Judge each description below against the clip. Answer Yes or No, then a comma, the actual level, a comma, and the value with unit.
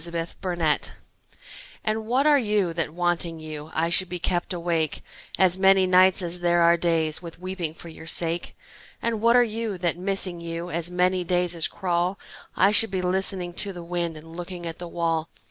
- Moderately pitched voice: Yes, medium, 175 Hz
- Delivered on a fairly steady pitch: Yes, narrow, 2.0 semitones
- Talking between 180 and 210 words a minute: Yes, average, 195 wpm